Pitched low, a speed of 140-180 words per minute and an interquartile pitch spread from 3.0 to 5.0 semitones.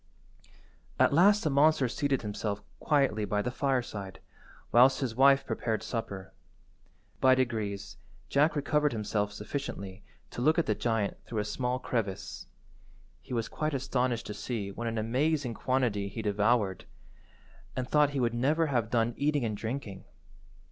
Yes: low, 120 Hz; average, 150 wpm; average, 4.7 semitones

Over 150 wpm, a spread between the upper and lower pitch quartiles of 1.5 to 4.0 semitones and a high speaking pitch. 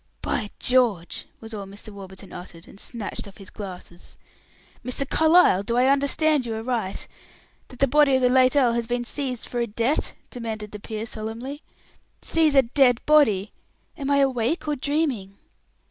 No: average, 170 wpm; average, 4.7 semitones; high, 240 Hz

